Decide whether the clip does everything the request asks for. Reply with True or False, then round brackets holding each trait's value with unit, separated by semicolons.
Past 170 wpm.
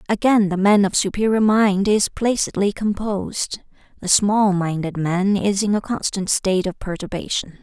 False (155 wpm)